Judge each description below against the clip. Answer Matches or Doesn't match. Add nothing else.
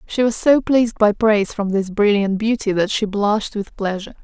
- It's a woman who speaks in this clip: Matches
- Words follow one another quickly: Matches